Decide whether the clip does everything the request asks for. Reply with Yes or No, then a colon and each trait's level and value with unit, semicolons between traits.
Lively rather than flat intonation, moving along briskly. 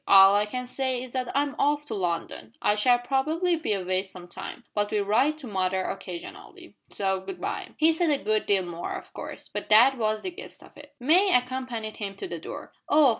Yes: wide, 6.3 semitones; fast, 220 wpm